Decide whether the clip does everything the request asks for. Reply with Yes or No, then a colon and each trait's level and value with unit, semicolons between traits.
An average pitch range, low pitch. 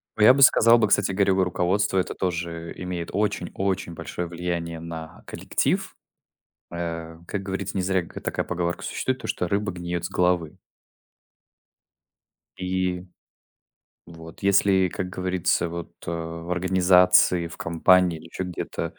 No: narrow, 1.9 semitones; very low, 90 Hz